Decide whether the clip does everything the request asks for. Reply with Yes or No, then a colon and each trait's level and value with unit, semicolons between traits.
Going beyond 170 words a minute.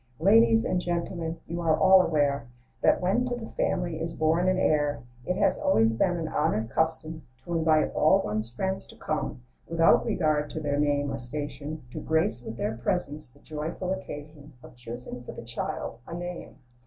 Yes: average, 190 wpm